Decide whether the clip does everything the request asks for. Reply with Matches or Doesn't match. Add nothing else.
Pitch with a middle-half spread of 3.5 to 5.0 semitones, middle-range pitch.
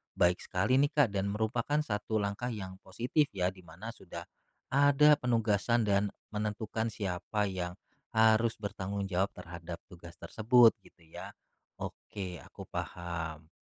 Doesn't match